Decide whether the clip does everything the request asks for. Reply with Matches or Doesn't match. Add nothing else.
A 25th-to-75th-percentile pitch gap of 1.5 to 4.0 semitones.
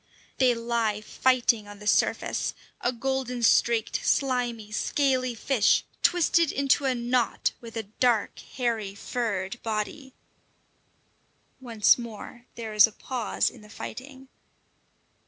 Matches